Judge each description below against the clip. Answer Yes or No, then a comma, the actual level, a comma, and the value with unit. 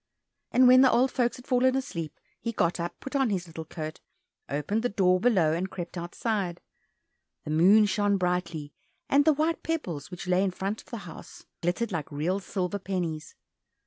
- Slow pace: No, average, 185 wpm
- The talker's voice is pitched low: No, high, 190 Hz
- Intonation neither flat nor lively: No, wide, 5.7 semitones